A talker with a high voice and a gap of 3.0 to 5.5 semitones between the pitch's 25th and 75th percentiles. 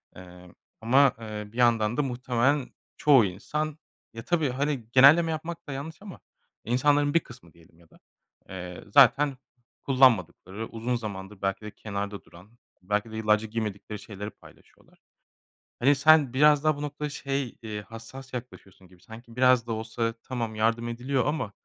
No: low, 120 Hz; average, 4.7 semitones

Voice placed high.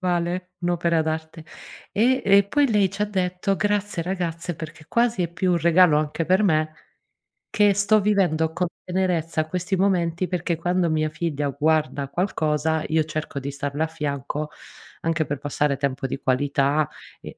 No: medium, 165 Hz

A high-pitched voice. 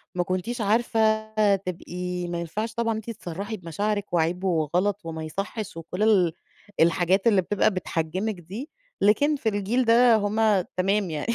Yes: high, 195 Hz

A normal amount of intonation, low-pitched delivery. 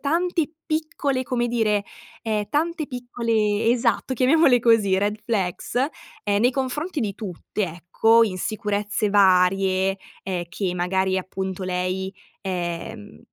No: average, 4.7 semitones; high, 210 Hz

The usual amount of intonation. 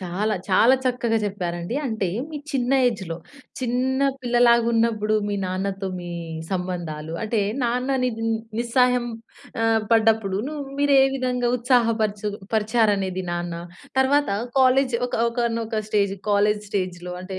Yes: average, 4.2 semitones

